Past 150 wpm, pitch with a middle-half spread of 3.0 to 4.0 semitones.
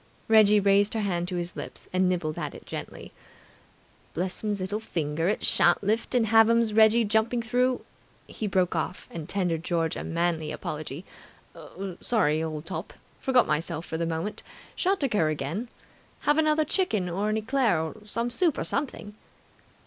No: average, 170 wpm; average, 5.1 semitones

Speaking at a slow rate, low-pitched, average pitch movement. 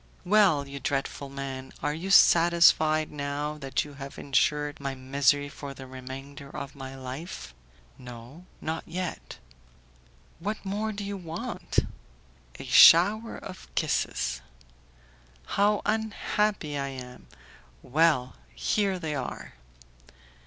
No: slow, 115 wpm; medium, 145 Hz; average, 4.7 semitones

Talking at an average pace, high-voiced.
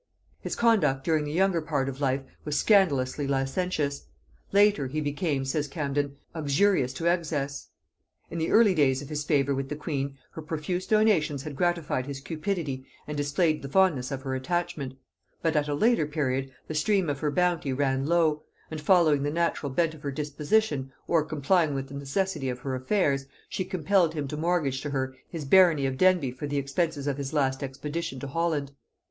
No: average, 190 wpm; medium, 150 Hz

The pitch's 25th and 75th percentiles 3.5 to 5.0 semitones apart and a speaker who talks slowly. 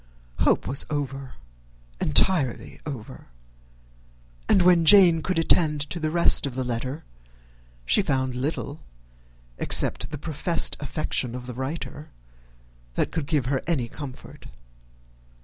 Yes: average, 3.9 semitones; slow, 125 wpm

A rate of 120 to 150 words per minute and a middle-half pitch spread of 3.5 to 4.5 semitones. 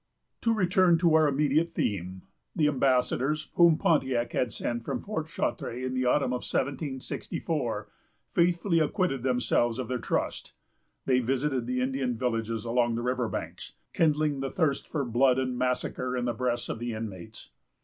No: average, 160 wpm; average, 4.0 semitones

